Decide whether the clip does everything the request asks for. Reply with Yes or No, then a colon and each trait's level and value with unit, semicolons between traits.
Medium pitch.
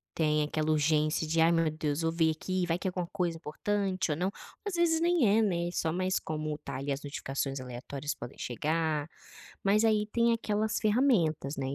Yes: medium, 165 Hz